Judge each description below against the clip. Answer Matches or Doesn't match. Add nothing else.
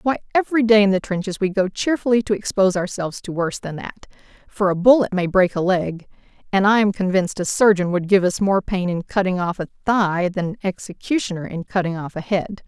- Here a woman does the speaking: Matches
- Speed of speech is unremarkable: Doesn't match